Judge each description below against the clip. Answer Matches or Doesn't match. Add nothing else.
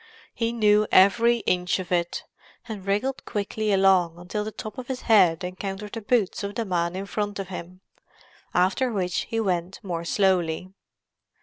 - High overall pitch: Matches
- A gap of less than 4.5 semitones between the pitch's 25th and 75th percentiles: Matches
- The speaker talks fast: Doesn't match